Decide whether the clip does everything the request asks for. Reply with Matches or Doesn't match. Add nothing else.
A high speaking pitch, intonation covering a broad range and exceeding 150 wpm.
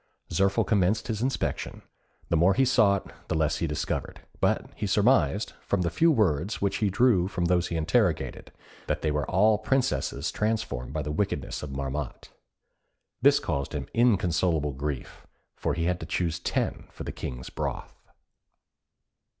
Doesn't match